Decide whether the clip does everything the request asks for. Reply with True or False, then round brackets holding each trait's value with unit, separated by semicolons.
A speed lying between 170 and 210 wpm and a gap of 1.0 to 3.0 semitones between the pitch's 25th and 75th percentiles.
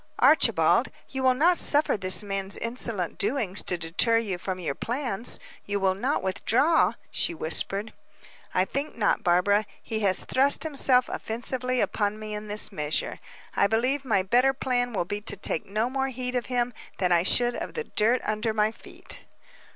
False (175 wpm; 4.5 semitones)